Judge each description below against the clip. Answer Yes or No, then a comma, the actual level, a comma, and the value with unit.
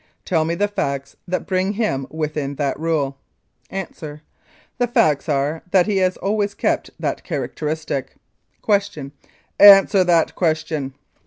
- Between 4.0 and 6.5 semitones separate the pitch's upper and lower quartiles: Yes, average, 5.0 semitones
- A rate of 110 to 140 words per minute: Yes, slow, 135 wpm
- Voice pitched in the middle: Yes, medium, 165 Hz